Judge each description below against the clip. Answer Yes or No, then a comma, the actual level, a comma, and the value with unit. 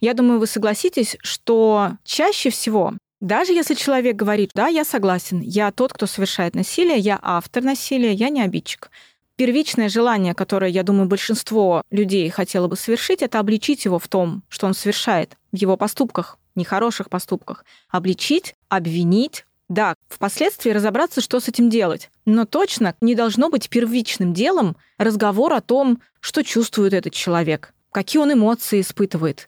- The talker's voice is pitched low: No, high, 215 Hz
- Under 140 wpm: No, average, 155 wpm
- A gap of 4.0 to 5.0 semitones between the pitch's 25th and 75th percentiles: Yes, average, 4.3 semitones